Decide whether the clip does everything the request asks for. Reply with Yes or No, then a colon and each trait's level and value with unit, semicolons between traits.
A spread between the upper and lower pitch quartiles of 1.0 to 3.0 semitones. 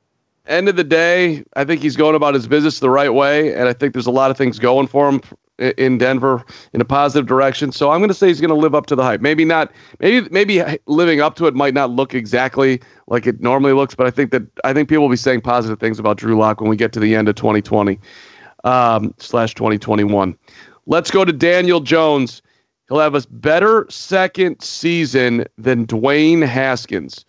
No: average, 4.1 semitones